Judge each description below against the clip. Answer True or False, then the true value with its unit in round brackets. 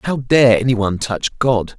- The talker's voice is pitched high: False (115 Hz)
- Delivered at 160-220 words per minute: True (200 wpm)